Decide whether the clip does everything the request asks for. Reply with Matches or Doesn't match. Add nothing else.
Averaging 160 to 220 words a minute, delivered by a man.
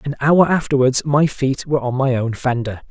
Matches